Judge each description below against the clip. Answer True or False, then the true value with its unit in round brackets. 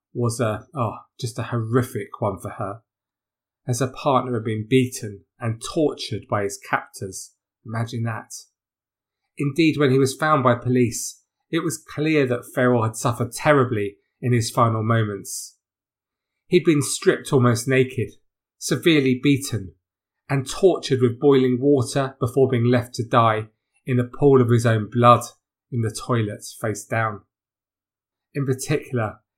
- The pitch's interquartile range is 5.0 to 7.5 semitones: False (3.3 semitones)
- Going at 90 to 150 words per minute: True (145 wpm)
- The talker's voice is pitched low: True (125 Hz)